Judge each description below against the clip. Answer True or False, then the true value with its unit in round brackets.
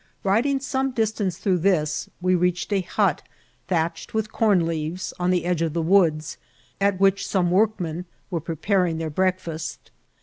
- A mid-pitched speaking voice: True (180 Hz)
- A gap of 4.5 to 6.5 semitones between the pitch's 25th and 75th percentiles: False (3.2 semitones)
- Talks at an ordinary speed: True (160 wpm)